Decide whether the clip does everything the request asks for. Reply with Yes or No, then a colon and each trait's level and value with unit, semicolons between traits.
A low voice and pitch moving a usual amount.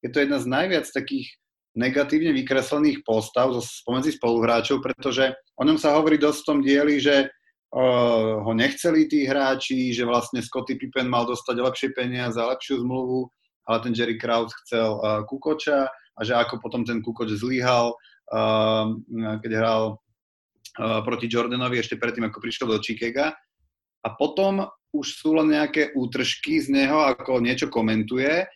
Yes: low, 125 Hz; average, 3.5 semitones